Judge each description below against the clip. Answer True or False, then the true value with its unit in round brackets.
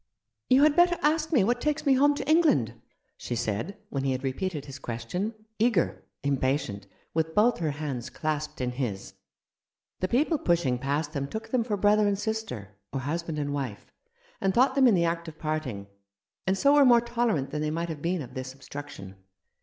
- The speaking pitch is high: False (160 Hz)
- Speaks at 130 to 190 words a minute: False (200 wpm)